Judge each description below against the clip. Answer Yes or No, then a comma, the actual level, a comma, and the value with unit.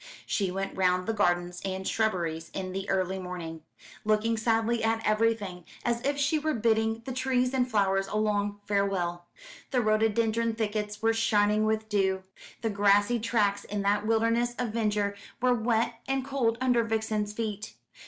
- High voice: Yes, high, 215 Hz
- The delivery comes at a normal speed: Yes, average, 165 wpm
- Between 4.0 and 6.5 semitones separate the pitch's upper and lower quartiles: No, narrow, 2.5 semitones